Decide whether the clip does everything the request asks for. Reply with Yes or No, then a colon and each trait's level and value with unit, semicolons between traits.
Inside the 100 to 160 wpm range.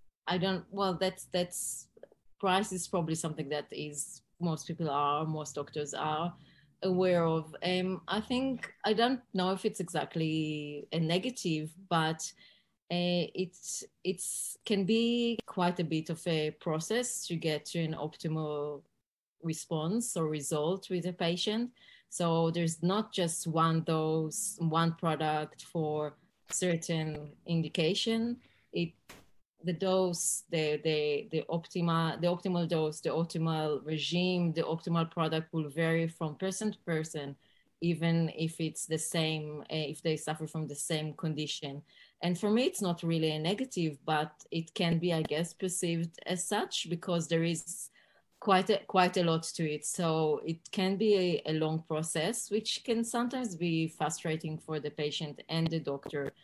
Yes: average, 155 wpm